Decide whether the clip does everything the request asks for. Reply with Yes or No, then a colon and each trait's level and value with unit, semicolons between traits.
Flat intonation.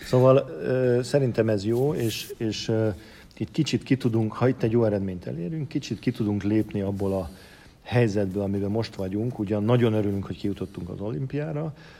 No: average, 3.8 semitones